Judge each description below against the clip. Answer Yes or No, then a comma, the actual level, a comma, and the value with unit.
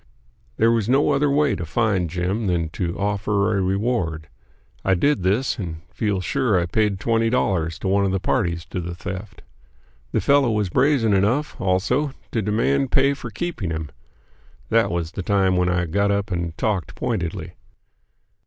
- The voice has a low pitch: Yes, low, 100 Hz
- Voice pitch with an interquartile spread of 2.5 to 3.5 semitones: No, average, 4.6 semitones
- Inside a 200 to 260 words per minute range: No, average, 175 wpm